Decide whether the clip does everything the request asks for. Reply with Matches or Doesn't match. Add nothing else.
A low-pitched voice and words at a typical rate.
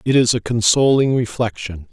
Matches